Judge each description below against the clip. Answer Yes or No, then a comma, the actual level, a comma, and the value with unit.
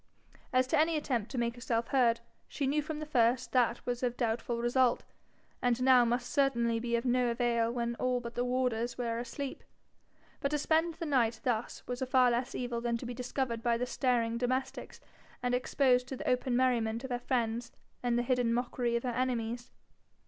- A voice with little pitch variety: Yes, narrow, 1.6 semitones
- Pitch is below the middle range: No, high, 245 Hz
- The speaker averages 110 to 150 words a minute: No, average, 200 wpm